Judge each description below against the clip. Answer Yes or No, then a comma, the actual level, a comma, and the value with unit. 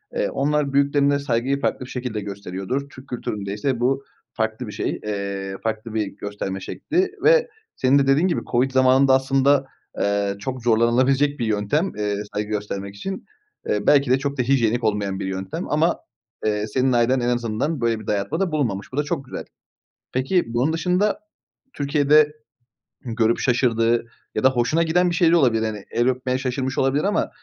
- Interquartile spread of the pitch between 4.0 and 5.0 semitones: Yes, average, 4.7 semitones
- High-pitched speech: No, low, 130 Hz